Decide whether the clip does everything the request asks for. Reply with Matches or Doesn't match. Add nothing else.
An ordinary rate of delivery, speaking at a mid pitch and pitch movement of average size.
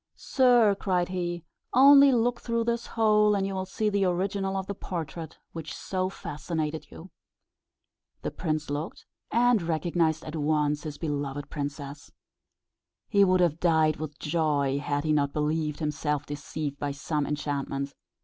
Matches